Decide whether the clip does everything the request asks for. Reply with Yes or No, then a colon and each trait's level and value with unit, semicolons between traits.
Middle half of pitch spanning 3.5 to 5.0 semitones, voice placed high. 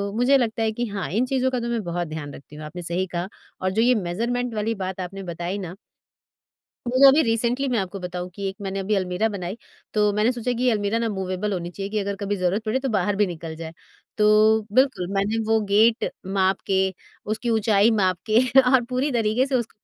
Yes: average, 3.9 semitones; high, 210 Hz